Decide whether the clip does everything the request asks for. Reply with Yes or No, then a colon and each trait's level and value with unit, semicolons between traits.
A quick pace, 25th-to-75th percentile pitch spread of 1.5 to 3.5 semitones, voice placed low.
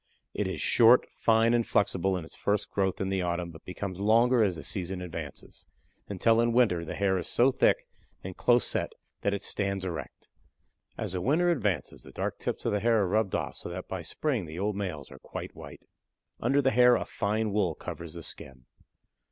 No: fast, 210 wpm; average, 4.3 semitones; low, 100 Hz